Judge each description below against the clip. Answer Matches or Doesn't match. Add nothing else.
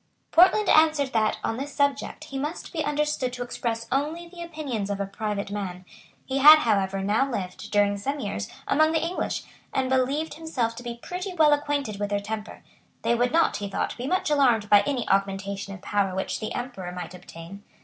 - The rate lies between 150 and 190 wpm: Doesn't match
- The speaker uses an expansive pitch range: Matches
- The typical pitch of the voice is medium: Doesn't match